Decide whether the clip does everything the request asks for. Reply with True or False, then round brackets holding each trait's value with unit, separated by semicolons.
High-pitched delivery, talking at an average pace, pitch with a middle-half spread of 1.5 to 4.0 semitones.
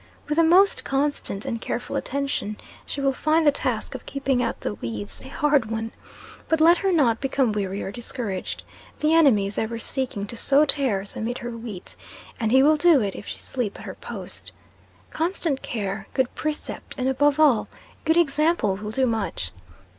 False (260 Hz; 185 wpm; 5.5 semitones)